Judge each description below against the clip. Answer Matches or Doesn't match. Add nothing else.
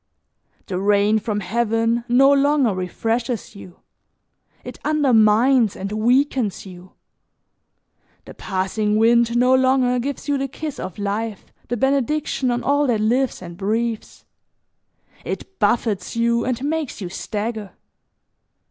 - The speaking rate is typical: Doesn't match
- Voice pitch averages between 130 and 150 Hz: Doesn't match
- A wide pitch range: Doesn't match